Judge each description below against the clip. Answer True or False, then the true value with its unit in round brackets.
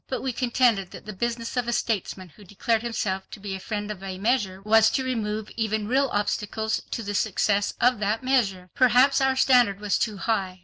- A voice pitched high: True (220 Hz)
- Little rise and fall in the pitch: False (3.2 semitones)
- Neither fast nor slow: False (210 wpm)